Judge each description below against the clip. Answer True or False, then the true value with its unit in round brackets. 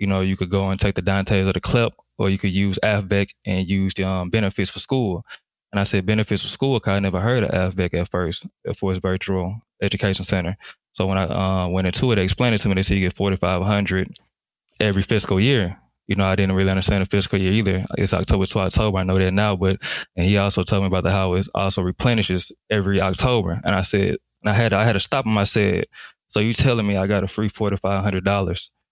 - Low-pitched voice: True (95 Hz)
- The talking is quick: True (255 wpm)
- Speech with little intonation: True (1.5 semitones)